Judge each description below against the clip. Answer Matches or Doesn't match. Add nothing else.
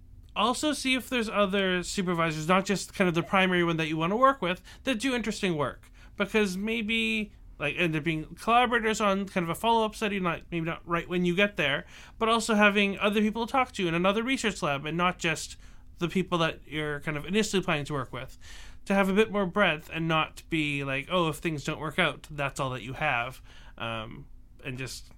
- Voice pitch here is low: Doesn't match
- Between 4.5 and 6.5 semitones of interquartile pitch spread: Matches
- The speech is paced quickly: Matches